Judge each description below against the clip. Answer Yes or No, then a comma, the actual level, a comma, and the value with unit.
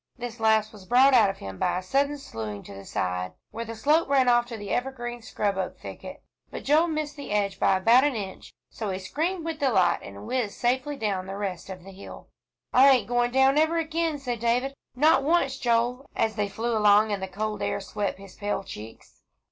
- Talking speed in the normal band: No, fast, 220 wpm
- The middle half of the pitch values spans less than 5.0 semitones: No, wide, 5.5 semitones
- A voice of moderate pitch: No, high, 230 Hz